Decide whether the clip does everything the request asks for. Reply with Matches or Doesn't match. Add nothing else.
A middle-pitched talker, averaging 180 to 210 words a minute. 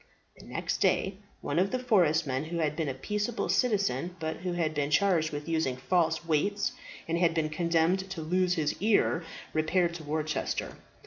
Matches